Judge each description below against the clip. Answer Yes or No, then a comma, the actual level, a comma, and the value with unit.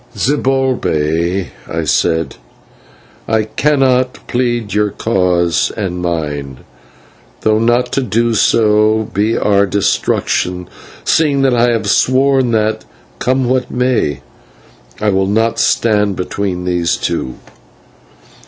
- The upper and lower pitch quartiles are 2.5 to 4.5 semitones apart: No, wide, 5.5 semitones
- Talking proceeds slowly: Yes, slow, 110 wpm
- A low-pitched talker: Yes, low, 110 Hz